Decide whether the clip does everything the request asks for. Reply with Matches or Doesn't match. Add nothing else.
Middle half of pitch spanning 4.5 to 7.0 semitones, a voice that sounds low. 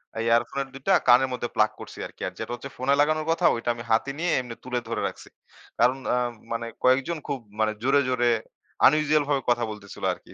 Doesn't match